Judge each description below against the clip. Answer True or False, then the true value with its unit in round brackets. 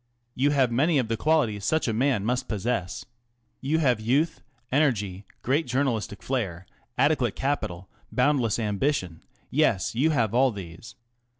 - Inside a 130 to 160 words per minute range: False (170 wpm)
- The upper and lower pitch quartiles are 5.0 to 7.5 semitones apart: True (5.3 semitones)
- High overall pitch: False (120 Hz)